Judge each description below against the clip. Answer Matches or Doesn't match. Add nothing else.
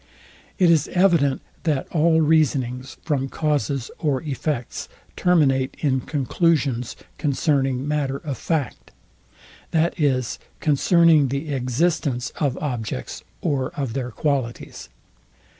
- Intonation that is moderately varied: Matches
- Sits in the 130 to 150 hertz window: Matches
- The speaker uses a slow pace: Matches